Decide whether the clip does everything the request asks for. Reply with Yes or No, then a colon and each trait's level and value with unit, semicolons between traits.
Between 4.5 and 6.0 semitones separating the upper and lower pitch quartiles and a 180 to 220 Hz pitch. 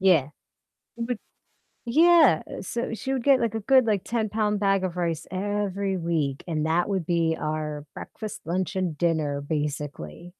Yes: average, 5.3 semitones; medium, 185 Hz